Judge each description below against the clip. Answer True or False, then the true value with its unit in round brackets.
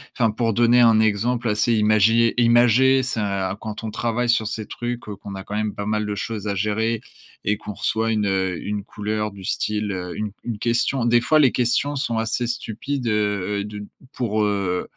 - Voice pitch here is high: False (110 Hz)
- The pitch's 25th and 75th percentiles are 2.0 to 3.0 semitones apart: True (2.4 semitones)